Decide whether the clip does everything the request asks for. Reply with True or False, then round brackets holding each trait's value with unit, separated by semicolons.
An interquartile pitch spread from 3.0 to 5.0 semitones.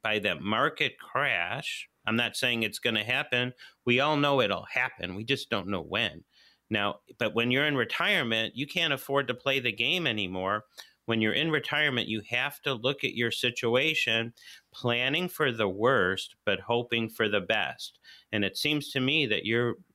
True (3.8 semitones)